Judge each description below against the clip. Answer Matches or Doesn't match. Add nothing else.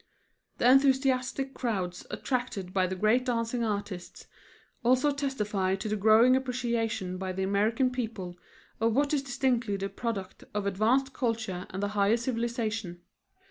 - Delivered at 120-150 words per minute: Matches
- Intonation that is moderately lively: Matches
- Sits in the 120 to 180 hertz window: Doesn't match